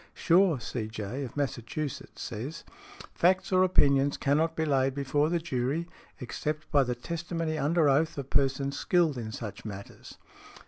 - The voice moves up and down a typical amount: Yes, average, 4.1 semitones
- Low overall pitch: No, medium, 145 Hz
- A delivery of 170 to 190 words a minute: No, average, 145 wpm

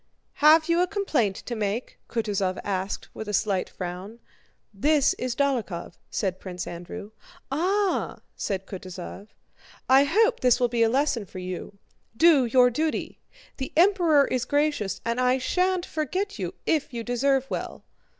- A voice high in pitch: Yes, very high, 250 Hz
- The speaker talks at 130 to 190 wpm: Yes, average, 150 wpm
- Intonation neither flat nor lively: No, wide, 7.2 semitones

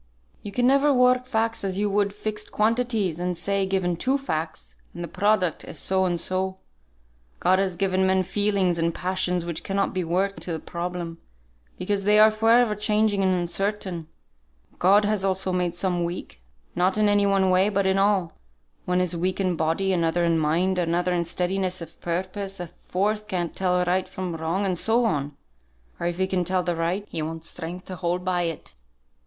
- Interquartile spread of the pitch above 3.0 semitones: No, narrow, 2.6 semitones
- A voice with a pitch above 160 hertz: Yes, medium, 185 Hz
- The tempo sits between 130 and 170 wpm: No, average, 195 wpm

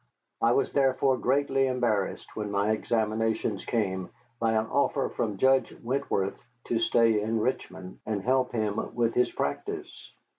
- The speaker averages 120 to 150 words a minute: Yes, average, 145 wpm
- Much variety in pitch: No, average, 3.3 semitones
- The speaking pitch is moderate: No, low, 115 Hz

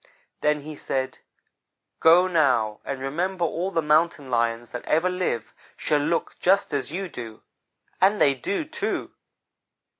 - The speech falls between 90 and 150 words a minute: Yes, average, 145 wpm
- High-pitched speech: No, medium, 150 Hz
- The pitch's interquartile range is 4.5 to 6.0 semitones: Yes, wide, 5.4 semitones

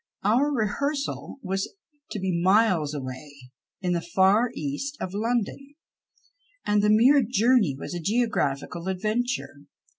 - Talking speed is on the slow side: Yes, slow, 125 wpm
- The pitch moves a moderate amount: No, wide, 6.1 semitones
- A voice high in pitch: Yes, high, 205 Hz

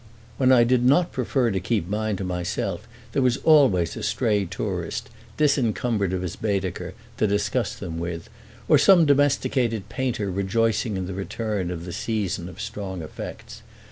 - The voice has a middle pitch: No, low, 105 Hz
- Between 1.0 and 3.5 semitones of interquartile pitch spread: No, average, 4.7 semitones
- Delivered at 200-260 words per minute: No, average, 165 wpm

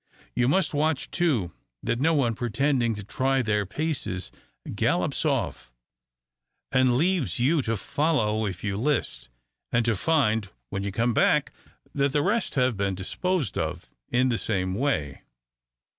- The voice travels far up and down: Yes, wide, 5.7 semitones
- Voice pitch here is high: No, low, 120 Hz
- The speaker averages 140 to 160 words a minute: Yes, average, 150 wpm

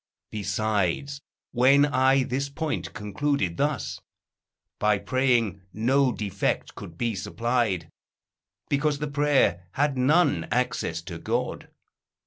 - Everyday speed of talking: No, slow, 110 wpm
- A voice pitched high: No, low, 125 Hz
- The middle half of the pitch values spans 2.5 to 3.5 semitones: No, wide, 5.5 semitones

